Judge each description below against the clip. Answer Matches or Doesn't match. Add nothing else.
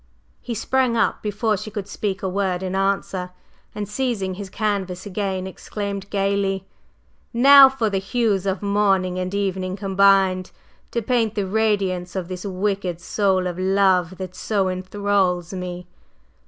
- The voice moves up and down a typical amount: Doesn't match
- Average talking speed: Matches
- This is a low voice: Doesn't match